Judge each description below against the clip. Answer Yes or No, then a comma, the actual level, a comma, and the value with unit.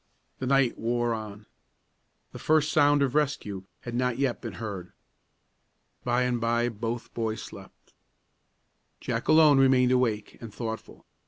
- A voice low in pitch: Yes, low, 120 Hz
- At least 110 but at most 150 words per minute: Yes, average, 140 wpm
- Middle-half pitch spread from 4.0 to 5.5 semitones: No, average, 3.0 semitones